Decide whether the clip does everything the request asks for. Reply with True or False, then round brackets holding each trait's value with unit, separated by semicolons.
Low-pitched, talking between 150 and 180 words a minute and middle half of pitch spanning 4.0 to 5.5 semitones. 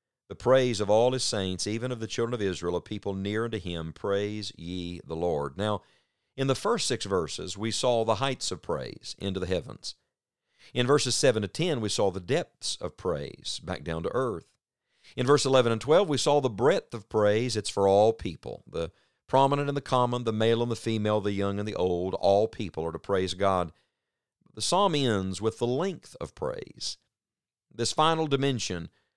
False (110 Hz; 200 wpm; 4.6 semitones)